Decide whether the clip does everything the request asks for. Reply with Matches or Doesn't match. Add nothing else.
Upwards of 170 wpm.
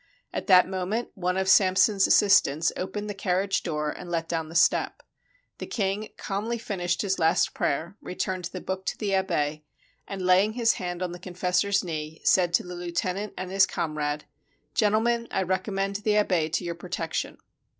Matches